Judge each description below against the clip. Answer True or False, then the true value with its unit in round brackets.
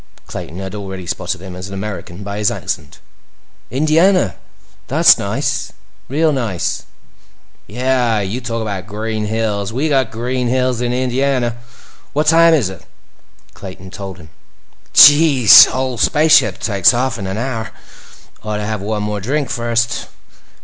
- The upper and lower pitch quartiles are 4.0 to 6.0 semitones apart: True (4.4 semitones)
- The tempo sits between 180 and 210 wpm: False (150 wpm)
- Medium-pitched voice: False (115 Hz)